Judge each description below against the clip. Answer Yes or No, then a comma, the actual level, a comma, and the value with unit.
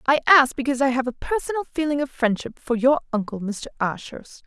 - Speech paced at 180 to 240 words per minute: Yes, average, 200 wpm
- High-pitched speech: Yes, very high, 260 Hz